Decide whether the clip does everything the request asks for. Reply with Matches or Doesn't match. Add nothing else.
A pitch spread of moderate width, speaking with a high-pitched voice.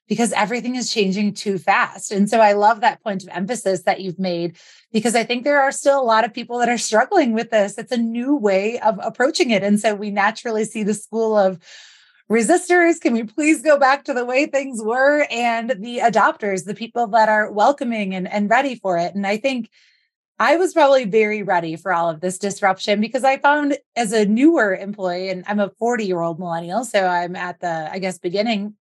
Matches